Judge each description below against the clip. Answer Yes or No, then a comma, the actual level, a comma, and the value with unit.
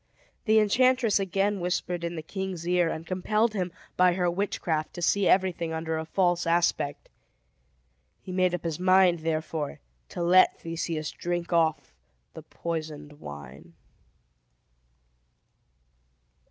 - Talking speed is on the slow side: Yes, slow, 125 wpm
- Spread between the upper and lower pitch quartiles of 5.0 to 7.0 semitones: No, narrow, 2.6 semitones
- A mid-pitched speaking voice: Yes, medium, 175 Hz